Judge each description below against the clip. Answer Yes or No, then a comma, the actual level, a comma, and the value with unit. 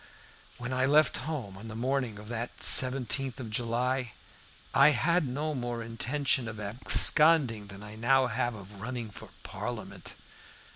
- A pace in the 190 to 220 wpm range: No, average, 150 wpm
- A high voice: No, low, 125 Hz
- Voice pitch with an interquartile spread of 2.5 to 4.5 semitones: Yes, average, 3.2 semitones